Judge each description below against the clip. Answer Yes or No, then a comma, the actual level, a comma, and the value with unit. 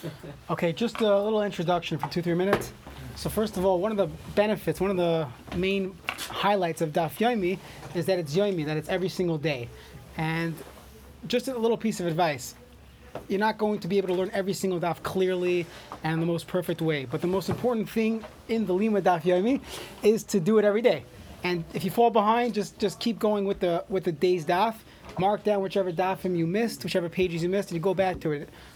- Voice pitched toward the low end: No, medium, 185 Hz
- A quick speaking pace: Yes, fast, 220 wpm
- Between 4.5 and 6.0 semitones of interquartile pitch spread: No, average, 3.4 semitones